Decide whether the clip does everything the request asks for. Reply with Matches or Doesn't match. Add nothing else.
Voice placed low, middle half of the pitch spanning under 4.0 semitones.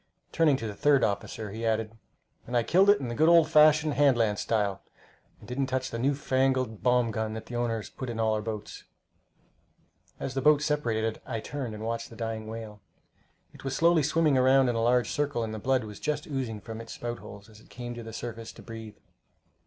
Matches